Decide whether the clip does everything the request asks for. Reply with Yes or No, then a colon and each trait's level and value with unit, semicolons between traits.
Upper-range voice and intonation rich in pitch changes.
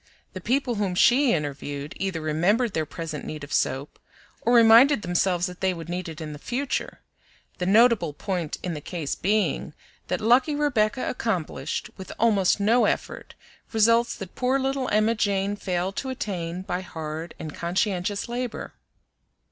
Yes: high, 195 Hz; wide, 5.7 semitones